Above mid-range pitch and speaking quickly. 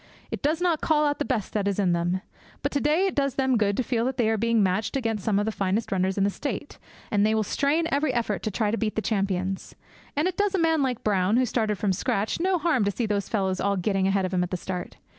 Yes: high, 220 Hz; fast, 280 wpm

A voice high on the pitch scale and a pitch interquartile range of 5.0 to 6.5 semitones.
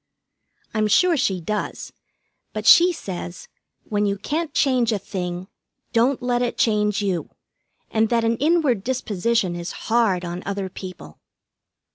No: high, 215 Hz; average, 4.5 semitones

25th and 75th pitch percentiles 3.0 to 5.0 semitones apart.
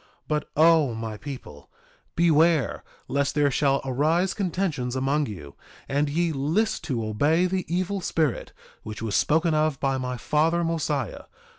Yes: average, 4.1 semitones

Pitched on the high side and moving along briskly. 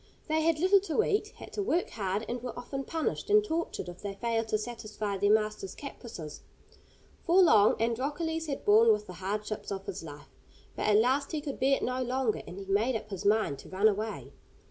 Yes: high, 225 Hz; fast, 210 wpm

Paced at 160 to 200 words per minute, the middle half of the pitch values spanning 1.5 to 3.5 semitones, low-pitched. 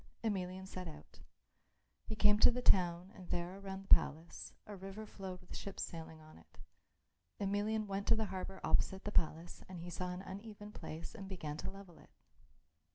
No: average, 190 wpm; average, 2.7 semitones; high, 190 Hz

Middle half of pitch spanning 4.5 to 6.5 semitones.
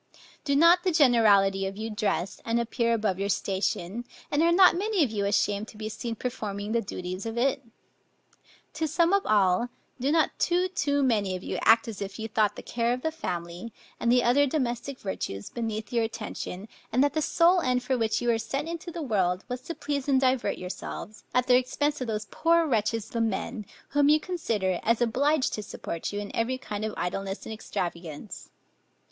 Yes: wide, 5.5 semitones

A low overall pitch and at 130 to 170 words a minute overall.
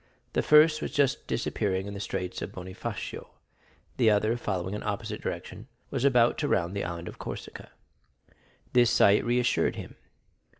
Yes: low, 110 Hz; average, 160 wpm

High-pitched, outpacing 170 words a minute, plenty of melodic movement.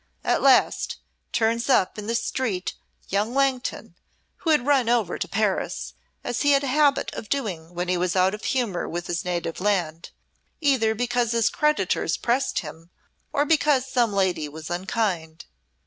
No: high, 220 Hz; average, 165 wpm; wide, 6.6 semitones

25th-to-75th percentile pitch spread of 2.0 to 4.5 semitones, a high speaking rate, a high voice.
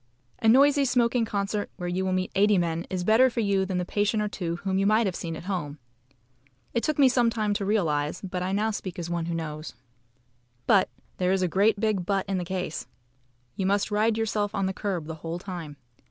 Yes: average, 3.3 semitones; fast, 225 wpm; high, 195 Hz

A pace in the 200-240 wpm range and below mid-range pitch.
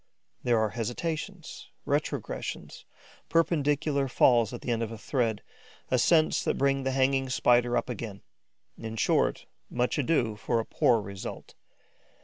No: slow, 135 wpm; low, 125 Hz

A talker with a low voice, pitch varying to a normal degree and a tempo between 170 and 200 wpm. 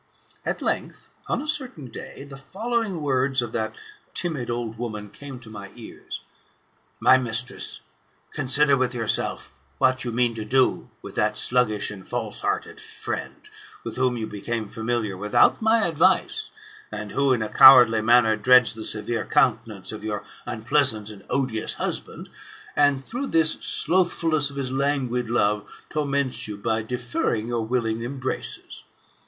No: low, 125 Hz; average, 4.0 semitones; average, 150 wpm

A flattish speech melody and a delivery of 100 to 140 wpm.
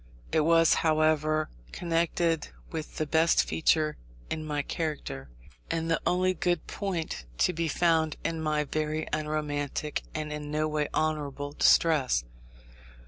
Yes: narrow, 1.5 semitones; slow, 135 wpm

